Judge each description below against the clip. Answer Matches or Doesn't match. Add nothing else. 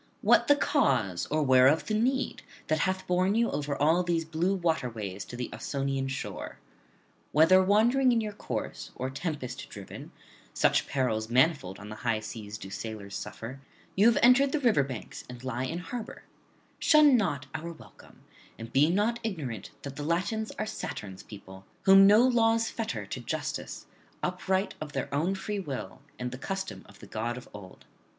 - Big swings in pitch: Matches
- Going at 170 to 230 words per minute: Matches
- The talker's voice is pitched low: Doesn't match